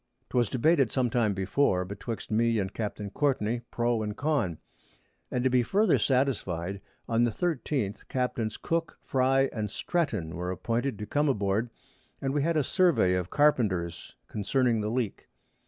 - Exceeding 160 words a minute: No, average, 155 wpm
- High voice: No, low, 120 Hz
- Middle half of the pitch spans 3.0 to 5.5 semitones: Yes, average, 4.9 semitones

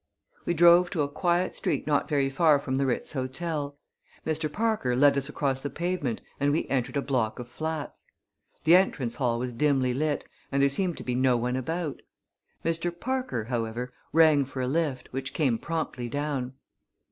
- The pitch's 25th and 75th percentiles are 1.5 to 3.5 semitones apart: No, average, 4.0 semitones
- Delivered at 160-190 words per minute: Yes, average, 180 wpm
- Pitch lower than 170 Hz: Yes, medium, 140 Hz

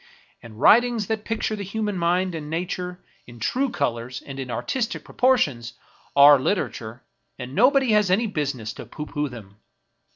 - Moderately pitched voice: Yes, medium, 170 Hz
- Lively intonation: Yes, wide, 9.0 semitones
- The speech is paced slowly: No, average, 165 wpm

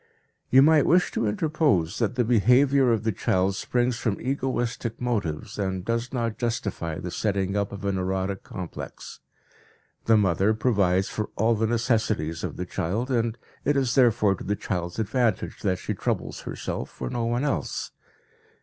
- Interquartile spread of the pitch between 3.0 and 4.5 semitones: Yes, average, 4.2 semitones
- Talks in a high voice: No, low, 110 Hz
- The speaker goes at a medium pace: Yes, average, 170 wpm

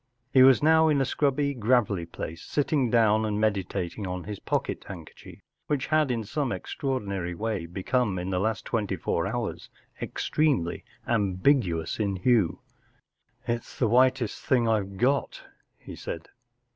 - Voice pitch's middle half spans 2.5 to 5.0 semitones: No, wide, 5.5 semitones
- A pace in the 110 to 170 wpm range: Yes, average, 160 wpm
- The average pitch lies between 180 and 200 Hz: No, low, 110 Hz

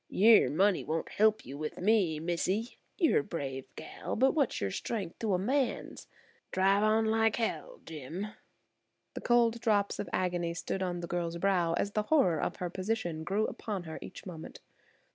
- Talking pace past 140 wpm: Yes, average, 180 wpm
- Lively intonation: No, average, 4.5 semitones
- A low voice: No, high, 190 Hz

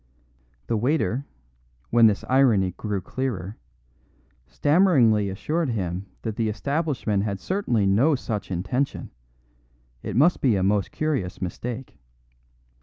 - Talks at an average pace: No, slow, 115 wpm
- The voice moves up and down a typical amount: No, wide, 5.8 semitones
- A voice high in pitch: No, low, 115 Hz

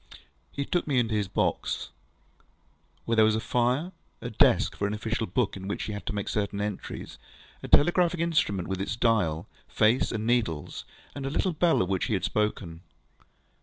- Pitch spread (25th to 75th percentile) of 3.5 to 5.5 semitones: Yes, average, 4.1 semitones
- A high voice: No, low, 110 Hz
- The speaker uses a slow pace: No, average, 190 wpm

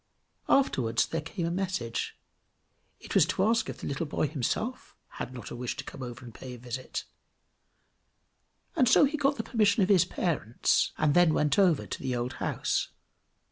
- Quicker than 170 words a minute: Yes, average, 180 wpm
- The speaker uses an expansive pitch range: Yes, wide, 7.9 semitones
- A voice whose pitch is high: No, medium, 155 Hz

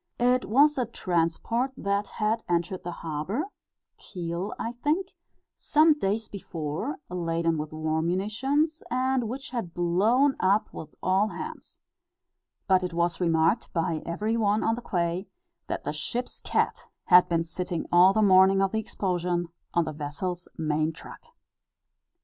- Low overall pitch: No, medium, 185 Hz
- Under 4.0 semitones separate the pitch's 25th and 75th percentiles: No, average, 5.2 semitones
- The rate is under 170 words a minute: Yes, average, 150 wpm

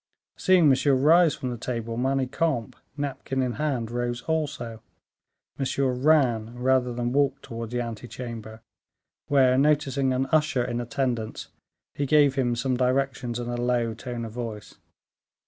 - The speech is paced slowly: No, average, 145 wpm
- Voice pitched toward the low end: Yes, low, 125 Hz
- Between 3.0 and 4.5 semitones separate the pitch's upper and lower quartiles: No, narrow, 2.5 semitones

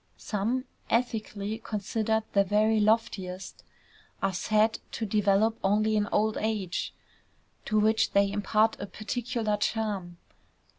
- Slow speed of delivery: Yes, slow, 115 wpm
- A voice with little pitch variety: Yes, narrow, 1.7 semitones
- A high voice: Yes, high, 215 Hz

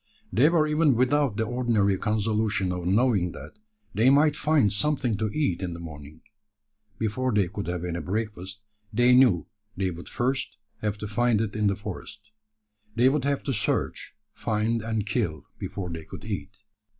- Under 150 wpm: No, average, 175 wpm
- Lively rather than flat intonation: No, average, 4.4 semitones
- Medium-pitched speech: No, low, 105 Hz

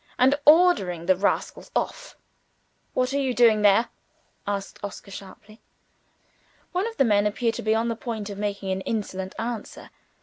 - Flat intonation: No, average, 3.7 semitones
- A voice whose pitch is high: Yes, high, 215 Hz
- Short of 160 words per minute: No, average, 165 wpm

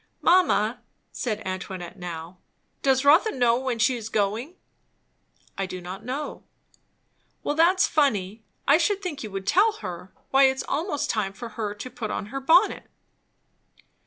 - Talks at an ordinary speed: Yes, average, 155 wpm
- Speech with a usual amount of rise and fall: No, wide, 6.8 semitones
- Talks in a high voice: Yes, high, 235 Hz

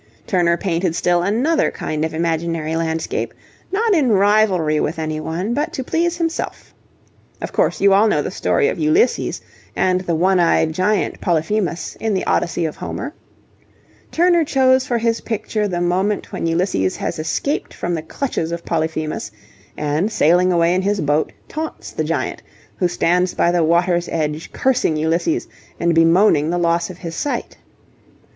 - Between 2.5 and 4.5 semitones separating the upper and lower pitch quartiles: No, average, 5.0 semitones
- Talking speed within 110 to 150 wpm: No, average, 165 wpm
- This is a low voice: No, medium, 175 Hz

